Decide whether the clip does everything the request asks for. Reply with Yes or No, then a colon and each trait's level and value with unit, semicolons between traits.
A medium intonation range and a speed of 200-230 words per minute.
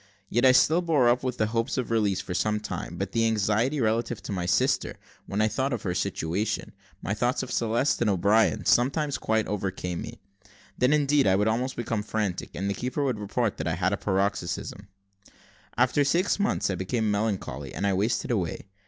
Yes: average, 4.0 semitones; fast, 205 wpm